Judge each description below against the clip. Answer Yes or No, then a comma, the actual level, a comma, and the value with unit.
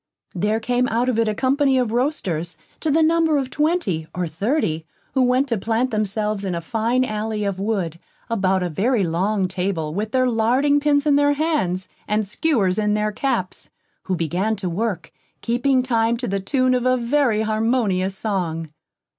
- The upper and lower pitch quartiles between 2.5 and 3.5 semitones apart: No, average, 5.1 semitones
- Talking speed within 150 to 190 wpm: Yes, average, 180 wpm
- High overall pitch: Yes, high, 220 Hz